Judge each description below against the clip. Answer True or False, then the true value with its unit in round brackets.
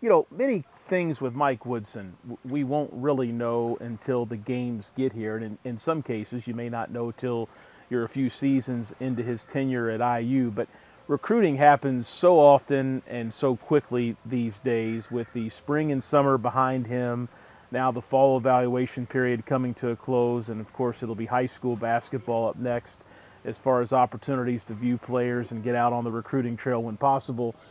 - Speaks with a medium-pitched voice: False (125 Hz)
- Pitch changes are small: True (2.1 semitones)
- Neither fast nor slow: True (190 wpm)